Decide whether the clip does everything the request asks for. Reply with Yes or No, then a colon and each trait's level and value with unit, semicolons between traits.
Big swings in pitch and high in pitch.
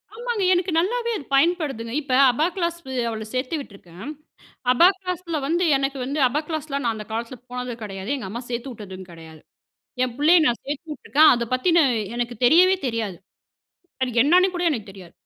Yes: wide, 6.8 semitones; very high, 270 Hz